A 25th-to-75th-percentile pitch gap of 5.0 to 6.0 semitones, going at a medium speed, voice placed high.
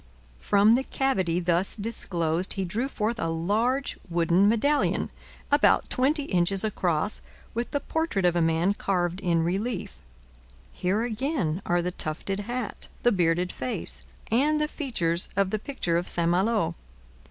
Yes: wide, 5.5 semitones; average, 150 wpm; high, 195 Hz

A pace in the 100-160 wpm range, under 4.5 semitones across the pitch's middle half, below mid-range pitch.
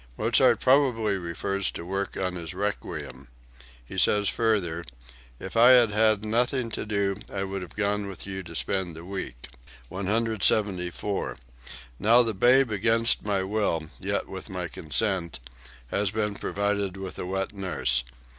Yes: average, 150 wpm; average, 2.8 semitones; low, 100 Hz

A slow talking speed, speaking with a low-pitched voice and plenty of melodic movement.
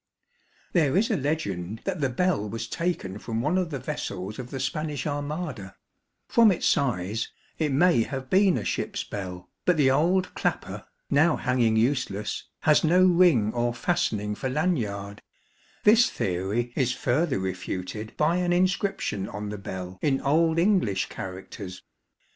No: average, 155 wpm; low, 130 Hz; wide, 8.3 semitones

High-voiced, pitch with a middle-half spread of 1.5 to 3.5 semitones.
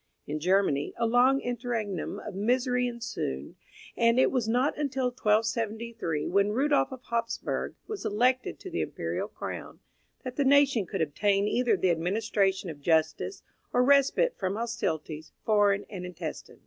No: high, 225 Hz; average, 4.6 semitones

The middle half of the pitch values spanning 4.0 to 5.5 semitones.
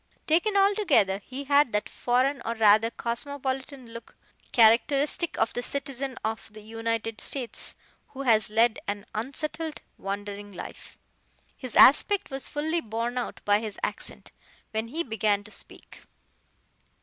Yes: average, 4.4 semitones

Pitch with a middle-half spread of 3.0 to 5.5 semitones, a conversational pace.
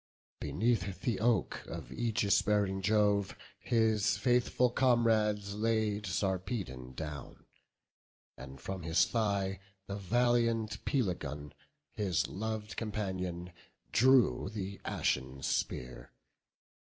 No: average, 3.9 semitones; slow, 95 wpm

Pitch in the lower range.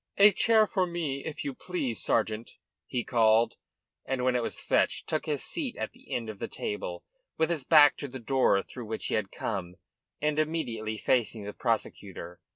Yes: low, 130 Hz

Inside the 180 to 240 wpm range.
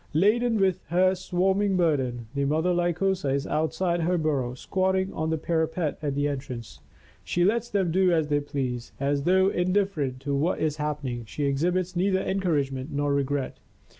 No: average, 170 wpm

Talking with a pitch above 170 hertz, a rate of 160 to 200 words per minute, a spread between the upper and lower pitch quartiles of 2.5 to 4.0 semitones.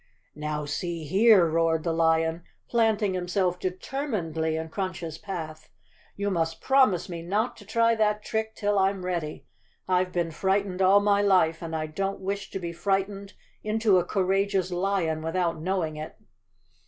Yes: medium, 185 Hz; average, 165 wpm; average, 3.5 semitones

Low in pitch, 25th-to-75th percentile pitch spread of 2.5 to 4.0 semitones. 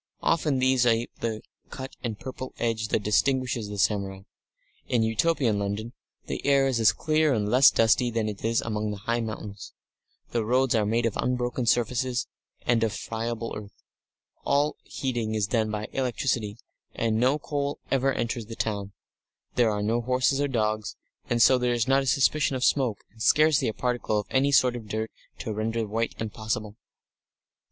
Yes: low, 115 Hz; average, 3.1 semitones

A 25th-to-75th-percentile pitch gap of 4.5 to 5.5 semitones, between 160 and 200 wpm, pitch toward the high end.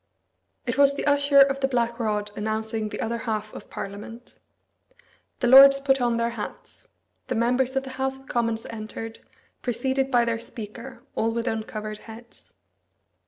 No: average, 3.2 semitones; average, 165 wpm; high, 235 Hz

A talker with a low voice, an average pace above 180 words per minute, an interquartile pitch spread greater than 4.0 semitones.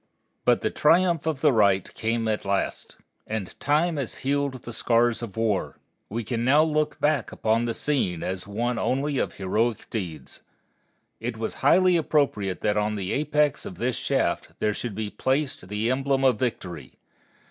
No: low, 120 Hz; average, 170 wpm; average, 5.2 semitones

